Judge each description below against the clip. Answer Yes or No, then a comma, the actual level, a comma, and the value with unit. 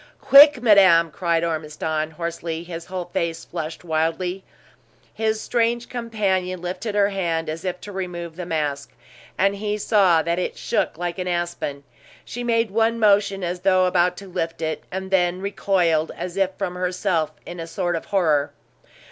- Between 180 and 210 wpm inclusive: No, average, 165 wpm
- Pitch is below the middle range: No, medium, 180 Hz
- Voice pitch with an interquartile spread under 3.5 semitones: Yes, average, 3.0 semitones